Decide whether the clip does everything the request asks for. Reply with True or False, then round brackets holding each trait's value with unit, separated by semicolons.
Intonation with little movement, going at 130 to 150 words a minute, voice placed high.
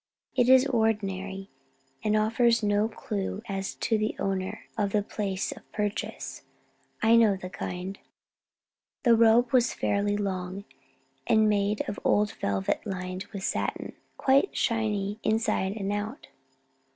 True (2.3 semitones; 135 wpm; 205 Hz)